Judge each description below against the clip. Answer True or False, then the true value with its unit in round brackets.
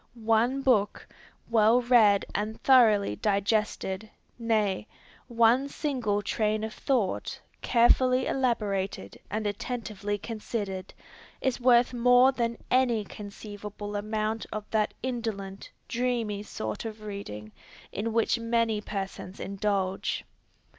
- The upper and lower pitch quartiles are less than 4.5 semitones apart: True (2.6 semitones)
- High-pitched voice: True (215 Hz)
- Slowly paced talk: True (105 wpm)